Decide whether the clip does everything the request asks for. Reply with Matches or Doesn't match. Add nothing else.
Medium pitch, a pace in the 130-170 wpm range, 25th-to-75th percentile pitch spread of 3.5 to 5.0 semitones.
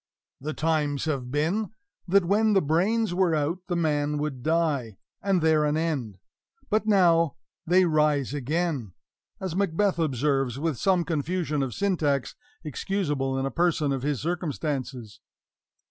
Matches